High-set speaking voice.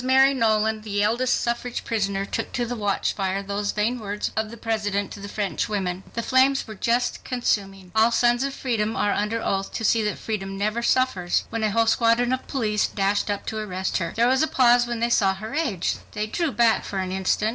Yes: high, 220 Hz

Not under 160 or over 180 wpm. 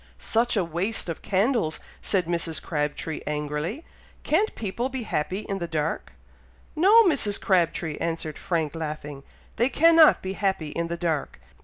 No: average, 150 wpm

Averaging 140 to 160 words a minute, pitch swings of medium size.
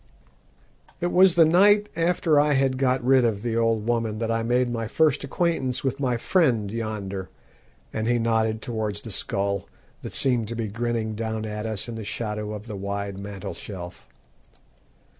No: average, 175 wpm; average, 3.5 semitones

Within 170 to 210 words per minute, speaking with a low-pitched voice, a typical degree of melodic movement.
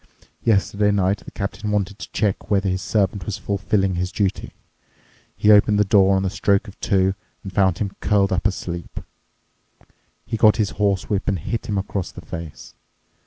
No: average, 175 wpm; low, 100 Hz; narrow, 1.6 semitones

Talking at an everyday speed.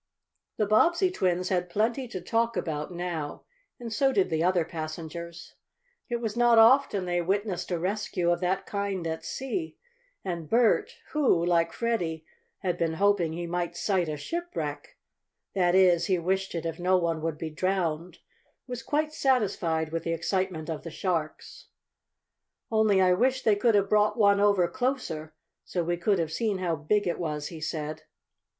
Yes: average, 170 wpm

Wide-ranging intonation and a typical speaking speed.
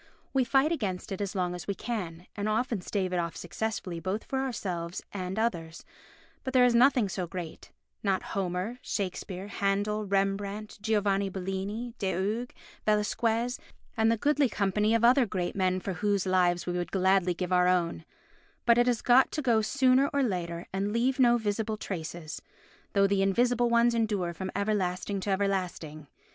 No: average, 4.1 semitones; average, 170 wpm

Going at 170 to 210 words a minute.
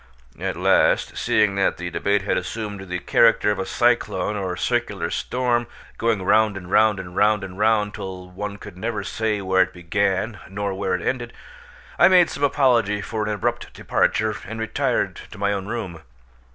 Yes: average, 180 wpm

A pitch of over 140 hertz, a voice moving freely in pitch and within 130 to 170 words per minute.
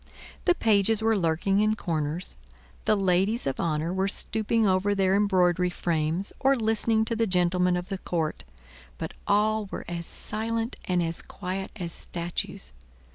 No: high, 190 Hz; average, 3.7 semitones; average, 155 wpm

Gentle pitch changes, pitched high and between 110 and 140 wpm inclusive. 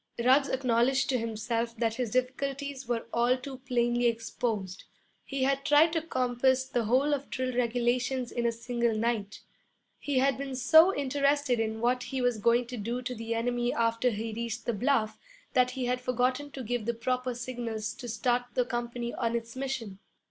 No: narrow, 2.0 semitones; high, 245 Hz; average, 185 wpm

